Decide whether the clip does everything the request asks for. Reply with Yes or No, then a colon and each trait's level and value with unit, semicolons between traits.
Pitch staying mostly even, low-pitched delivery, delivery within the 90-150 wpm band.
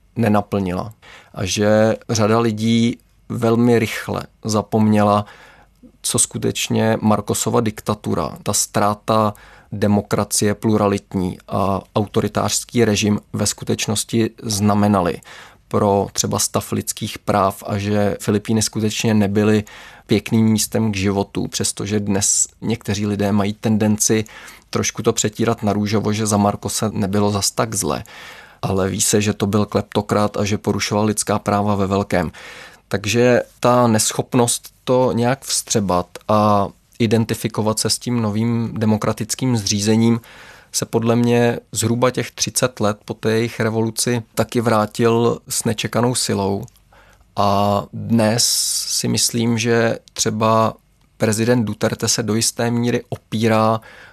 Yes: narrow, 2.0 semitones; low, 110 Hz; average, 125 wpm